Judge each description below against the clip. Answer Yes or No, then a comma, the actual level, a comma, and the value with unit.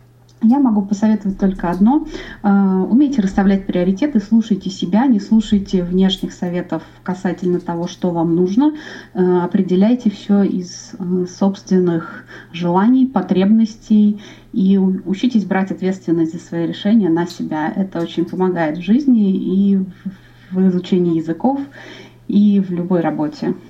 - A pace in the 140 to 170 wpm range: No, average, 120 wpm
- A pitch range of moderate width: Yes, average, 3.1 semitones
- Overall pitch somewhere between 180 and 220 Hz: Yes, high, 190 Hz